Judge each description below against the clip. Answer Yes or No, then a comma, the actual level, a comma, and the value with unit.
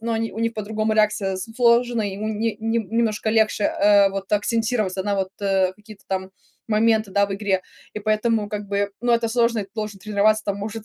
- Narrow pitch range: Yes, narrow, 1.9 semitones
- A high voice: Yes, high, 215 Hz